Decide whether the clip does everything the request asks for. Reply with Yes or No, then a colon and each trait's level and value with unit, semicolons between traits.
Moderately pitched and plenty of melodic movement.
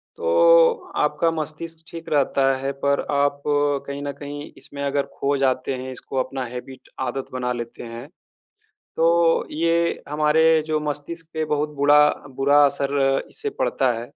No: medium, 145 Hz; average, 3.0 semitones